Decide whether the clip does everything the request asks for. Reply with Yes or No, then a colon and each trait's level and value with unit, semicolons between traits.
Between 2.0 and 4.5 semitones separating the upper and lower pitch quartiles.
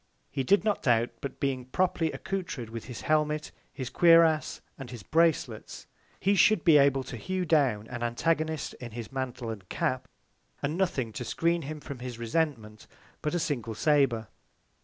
No: average, 5.3 semitones